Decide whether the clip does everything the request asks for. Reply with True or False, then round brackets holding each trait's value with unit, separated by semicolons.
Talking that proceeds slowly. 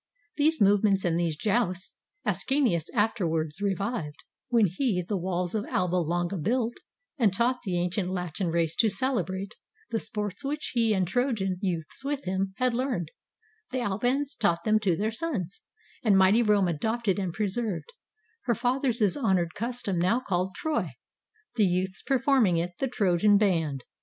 False (155 wpm)